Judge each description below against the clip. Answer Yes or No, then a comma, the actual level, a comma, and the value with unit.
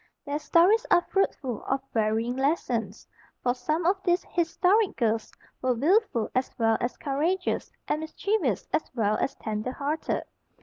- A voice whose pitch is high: Yes, very high, 280 Hz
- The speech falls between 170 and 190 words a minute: No, average, 145 wpm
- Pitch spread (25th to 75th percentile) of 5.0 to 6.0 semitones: No, wide, 7.0 semitones